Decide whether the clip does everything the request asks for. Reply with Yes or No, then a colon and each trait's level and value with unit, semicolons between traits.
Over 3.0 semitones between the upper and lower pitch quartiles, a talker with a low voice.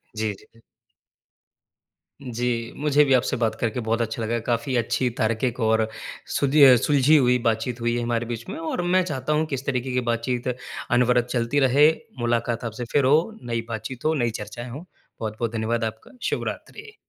No: narrow, 2.6 semitones; low, 120 Hz